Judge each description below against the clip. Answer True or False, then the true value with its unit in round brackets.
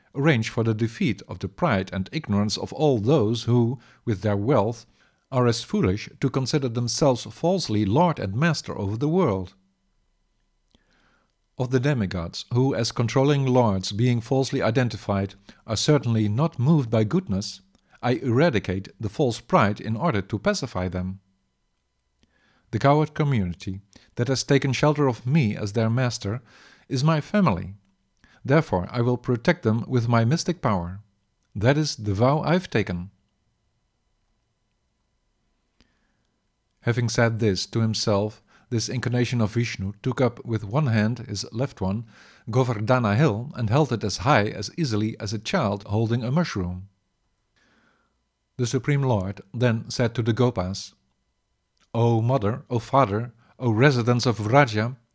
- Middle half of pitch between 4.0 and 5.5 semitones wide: True (4.5 semitones)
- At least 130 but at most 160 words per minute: True (145 wpm)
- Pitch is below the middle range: True (115 Hz)